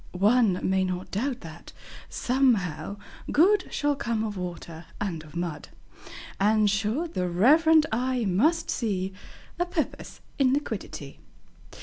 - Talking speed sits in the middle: No, slow, 125 wpm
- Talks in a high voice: Yes, high, 215 Hz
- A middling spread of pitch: No, wide, 6.8 semitones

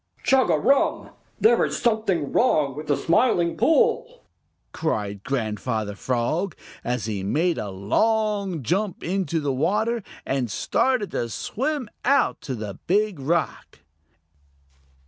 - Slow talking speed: Yes, slow, 120 wpm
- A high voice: No, medium, 170 Hz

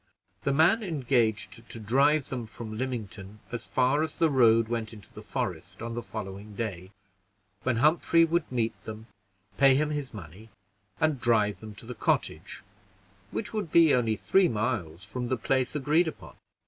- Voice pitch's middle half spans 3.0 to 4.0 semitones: No, average, 5.1 semitones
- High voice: No, low, 120 Hz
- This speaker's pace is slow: No, average, 170 wpm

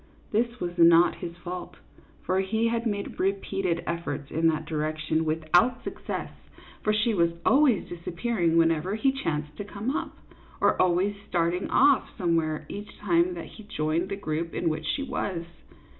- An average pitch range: Yes, average, 4.0 semitones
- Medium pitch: Yes, medium, 175 Hz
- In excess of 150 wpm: Yes, average, 170 wpm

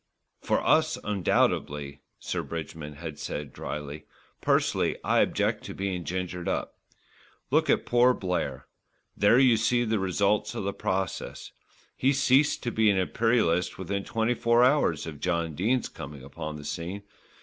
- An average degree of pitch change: No, wide, 5.7 semitones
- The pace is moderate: Yes, average, 150 wpm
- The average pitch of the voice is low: Yes, very low, 95 Hz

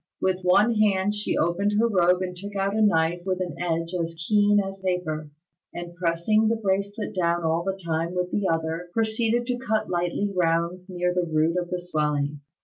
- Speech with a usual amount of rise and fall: Yes, average, 3.2 semitones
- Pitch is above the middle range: No, medium, 180 Hz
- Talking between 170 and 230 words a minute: Yes, average, 195 wpm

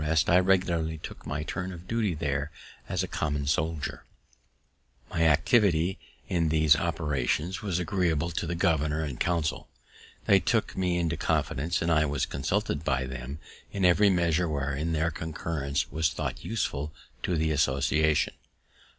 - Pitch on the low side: Yes, very low, 80 Hz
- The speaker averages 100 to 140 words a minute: No, average, 150 wpm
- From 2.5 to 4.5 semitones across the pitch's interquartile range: Yes, average, 2.8 semitones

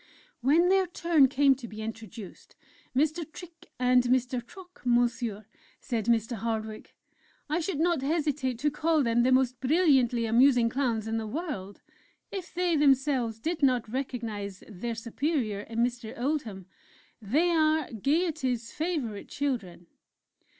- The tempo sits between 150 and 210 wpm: No, slow, 135 wpm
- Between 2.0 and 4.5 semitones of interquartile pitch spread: No, average, 5.2 semitones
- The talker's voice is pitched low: No, very high, 255 Hz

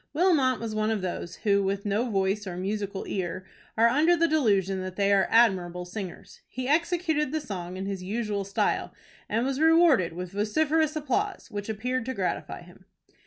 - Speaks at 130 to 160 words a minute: No, average, 180 wpm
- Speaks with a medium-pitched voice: No, high, 215 Hz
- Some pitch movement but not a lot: No, wide, 6.5 semitones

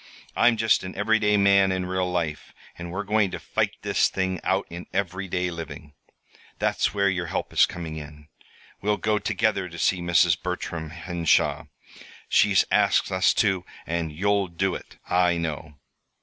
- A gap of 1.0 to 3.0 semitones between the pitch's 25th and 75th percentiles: Yes, average, 2.7 semitones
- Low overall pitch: Yes, very low, 90 Hz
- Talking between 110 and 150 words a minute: No, average, 165 wpm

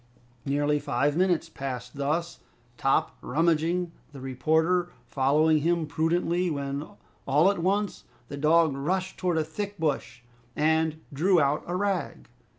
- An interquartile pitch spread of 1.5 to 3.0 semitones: No, average, 3.6 semitones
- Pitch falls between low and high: Yes, medium, 160 Hz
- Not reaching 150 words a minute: Yes, slow, 135 wpm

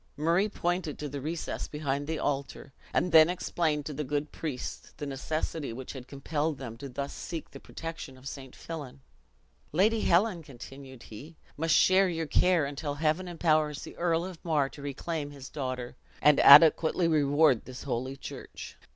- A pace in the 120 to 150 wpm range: No, average, 170 wpm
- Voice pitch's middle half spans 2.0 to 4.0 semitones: Yes, average, 3.1 semitones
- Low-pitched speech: No, medium, 150 Hz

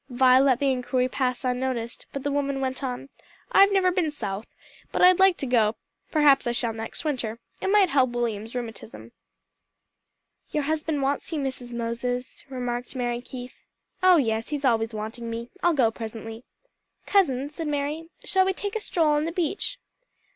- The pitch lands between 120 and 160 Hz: No, very high, 260 Hz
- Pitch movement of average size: Yes, average, 4.1 semitones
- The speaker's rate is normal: Yes, average, 175 wpm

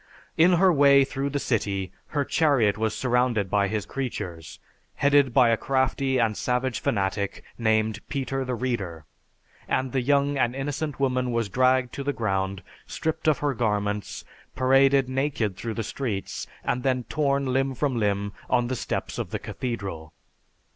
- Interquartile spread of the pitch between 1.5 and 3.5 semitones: No, average, 4.3 semitones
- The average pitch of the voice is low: Yes, low, 125 Hz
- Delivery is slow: No, average, 160 wpm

